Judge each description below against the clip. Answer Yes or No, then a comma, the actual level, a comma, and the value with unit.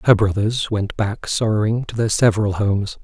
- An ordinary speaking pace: Yes, average, 180 wpm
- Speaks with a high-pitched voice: No, low, 105 Hz